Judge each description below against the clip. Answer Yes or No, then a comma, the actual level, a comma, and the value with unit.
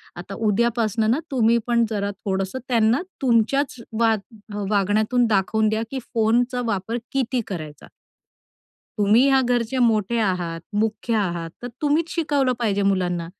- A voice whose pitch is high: Yes, high, 220 Hz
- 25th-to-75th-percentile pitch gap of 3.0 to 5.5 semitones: Yes, average, 3.5 semitones